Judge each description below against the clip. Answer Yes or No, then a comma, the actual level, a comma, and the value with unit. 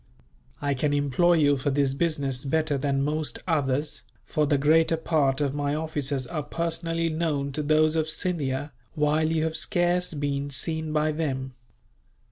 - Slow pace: No, average, 160 wpm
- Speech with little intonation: Yes, narrow, 2.2 semitones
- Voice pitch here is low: No, medium, 150 Hz